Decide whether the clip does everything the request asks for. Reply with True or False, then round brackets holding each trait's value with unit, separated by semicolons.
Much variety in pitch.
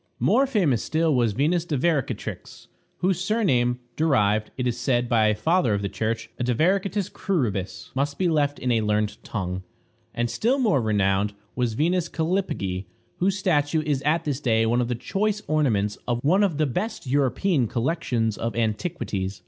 True (7.2 semitones)